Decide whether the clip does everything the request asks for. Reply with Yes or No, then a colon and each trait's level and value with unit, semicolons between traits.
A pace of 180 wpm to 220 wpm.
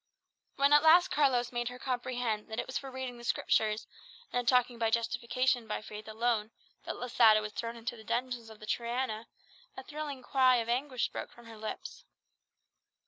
Yes: average, 185 wpm